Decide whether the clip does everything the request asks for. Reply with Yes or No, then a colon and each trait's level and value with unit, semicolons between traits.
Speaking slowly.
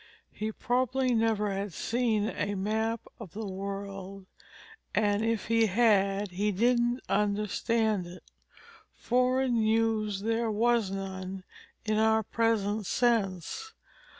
Yes: slow, 115 wpm